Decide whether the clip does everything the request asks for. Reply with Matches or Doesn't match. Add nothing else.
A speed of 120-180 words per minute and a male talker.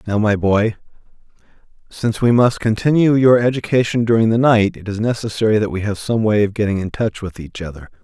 Doesn't match